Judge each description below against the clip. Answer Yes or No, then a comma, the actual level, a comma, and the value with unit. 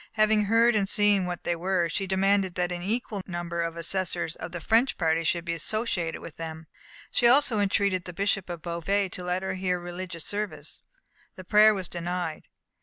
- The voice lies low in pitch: No, medium, 185 Hz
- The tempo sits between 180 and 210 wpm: Yes, average, 190 wpm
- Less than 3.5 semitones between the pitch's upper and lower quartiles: Yes, average, 2.9 semitones